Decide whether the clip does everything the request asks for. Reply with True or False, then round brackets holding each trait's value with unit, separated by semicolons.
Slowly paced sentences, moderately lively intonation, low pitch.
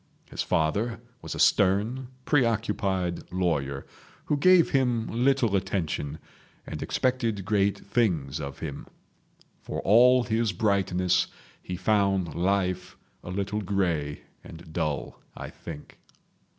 True (115 wpm; 4.9 semitones; 100 Hz)